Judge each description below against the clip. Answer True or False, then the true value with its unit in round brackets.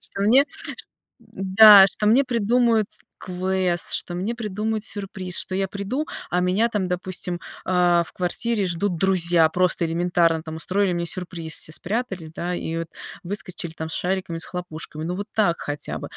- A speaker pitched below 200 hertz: True (185 Hz)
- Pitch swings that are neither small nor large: True (3.0 semitones)